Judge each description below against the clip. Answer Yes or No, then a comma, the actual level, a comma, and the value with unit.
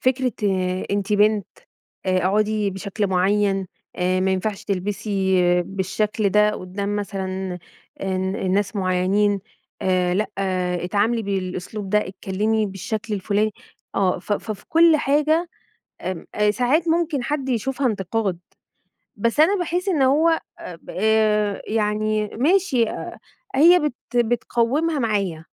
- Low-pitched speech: No, high, 210 Hz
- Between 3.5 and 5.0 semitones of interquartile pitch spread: Yes, average, 4.2 semitones